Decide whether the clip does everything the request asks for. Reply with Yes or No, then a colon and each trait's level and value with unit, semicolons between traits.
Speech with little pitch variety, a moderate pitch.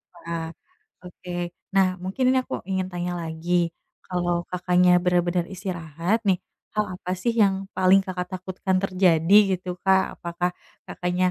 Yes: narrow, 1.3 semitones; medium, 180 Hz